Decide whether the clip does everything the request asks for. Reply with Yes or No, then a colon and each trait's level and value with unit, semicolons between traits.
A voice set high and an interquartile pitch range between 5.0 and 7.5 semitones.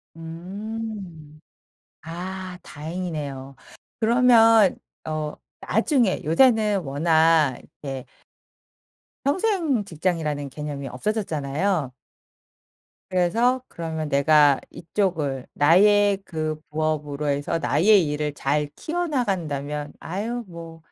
No: medium, 165 Hz; wide, 5.6 semitones